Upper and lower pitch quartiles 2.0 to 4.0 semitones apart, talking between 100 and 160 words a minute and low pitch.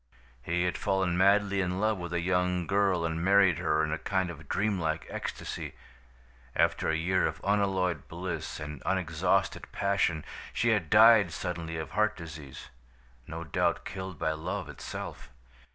Yes: average, 3.3 semitones; average, 155 wpm; very low, 90 Hz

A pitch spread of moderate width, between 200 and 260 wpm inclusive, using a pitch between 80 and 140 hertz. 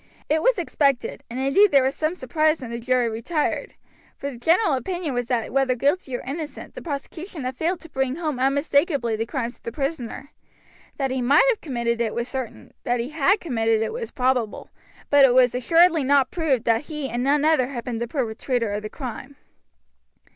No: average, 4.1 semitones; fast, 205 wpm; very high, 270 Hz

